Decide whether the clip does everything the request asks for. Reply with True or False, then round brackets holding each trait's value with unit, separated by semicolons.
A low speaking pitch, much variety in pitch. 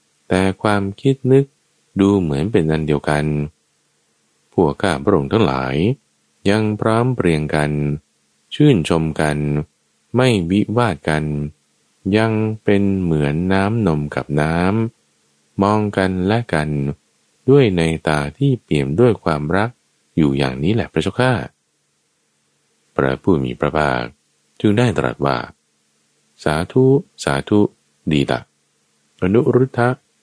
True (85 Hz; 6.7 semitones)